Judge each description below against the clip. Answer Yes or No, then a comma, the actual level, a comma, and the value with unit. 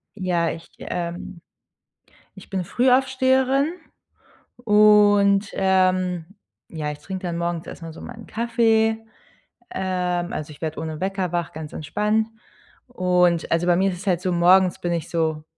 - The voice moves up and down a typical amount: Yes, average, 3.6 semitones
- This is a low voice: No, medium, 185 Hz